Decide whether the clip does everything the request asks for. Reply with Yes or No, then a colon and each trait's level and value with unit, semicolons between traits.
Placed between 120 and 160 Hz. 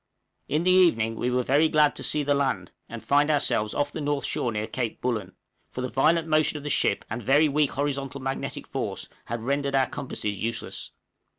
Yes: medium, 140 Hz